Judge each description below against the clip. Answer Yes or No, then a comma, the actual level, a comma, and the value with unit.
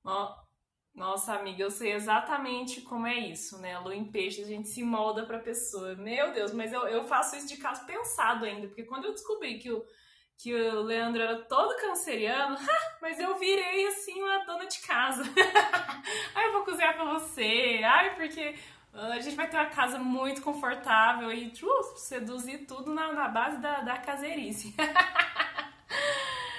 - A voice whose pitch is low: No, very high, 260 Hz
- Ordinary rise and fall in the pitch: No, wide, 6.2 semitones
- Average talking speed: Yes, average, 170 wpm